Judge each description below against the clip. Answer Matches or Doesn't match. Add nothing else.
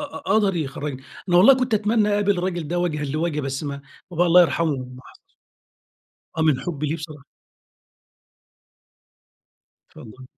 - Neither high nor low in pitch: Matches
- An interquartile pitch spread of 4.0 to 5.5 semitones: Matches